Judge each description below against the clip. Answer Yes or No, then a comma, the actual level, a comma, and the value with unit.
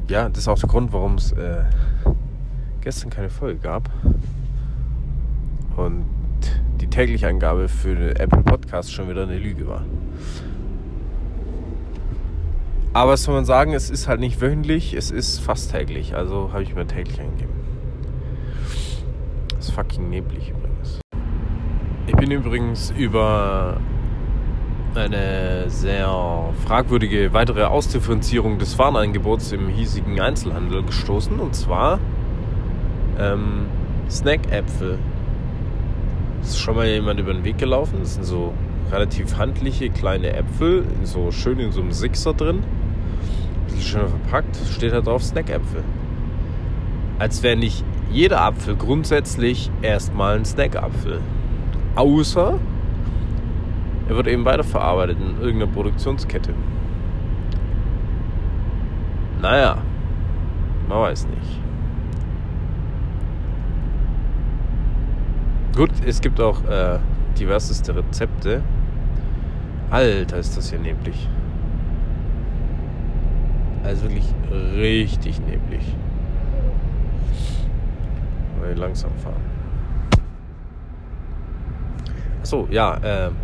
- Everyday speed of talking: No, slow, 100 wpm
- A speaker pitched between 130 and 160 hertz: No, very low, 95 Hz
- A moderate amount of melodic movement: Yes, average, 5.0 semitones